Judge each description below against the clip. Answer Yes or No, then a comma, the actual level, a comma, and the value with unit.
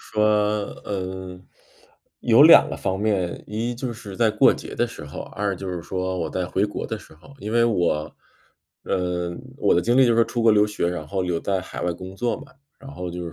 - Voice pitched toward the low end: Yes, very low, 95 Hz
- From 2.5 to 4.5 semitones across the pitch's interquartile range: Yes, average, 3.4 semitones